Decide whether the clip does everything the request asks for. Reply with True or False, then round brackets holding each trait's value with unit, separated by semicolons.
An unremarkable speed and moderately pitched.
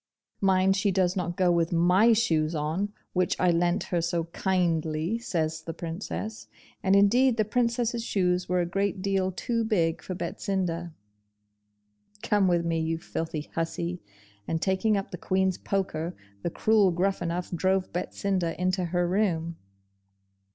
True (150 wpm; 180 Hz)